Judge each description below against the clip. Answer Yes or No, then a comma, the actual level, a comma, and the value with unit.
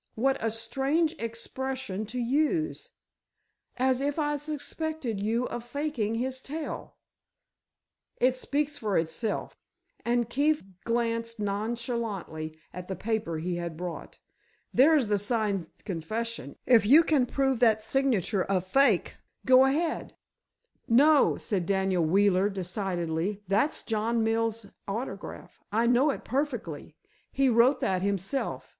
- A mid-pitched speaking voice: No, high, 230 Hz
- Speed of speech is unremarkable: No, slow, 120 wpm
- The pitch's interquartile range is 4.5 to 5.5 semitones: Yes, average, 5.2 semitones